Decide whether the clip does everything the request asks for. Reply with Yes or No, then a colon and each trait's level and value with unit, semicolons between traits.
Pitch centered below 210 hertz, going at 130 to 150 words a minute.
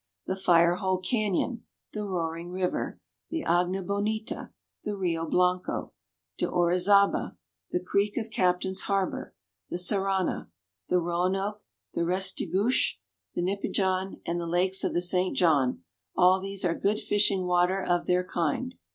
Yes: medium, 185 Hz; average, 140 wpm